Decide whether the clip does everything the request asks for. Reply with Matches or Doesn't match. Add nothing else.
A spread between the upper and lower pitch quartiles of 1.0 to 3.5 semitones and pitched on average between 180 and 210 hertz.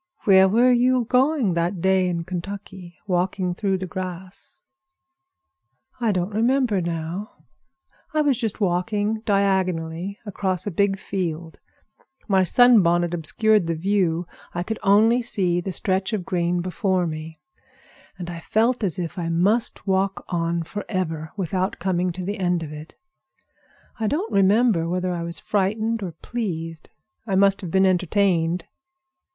Matches